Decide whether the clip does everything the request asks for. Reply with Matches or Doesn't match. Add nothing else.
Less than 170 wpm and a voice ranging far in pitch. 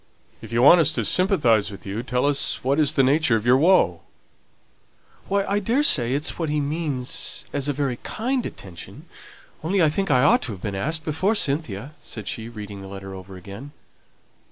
Doesn't match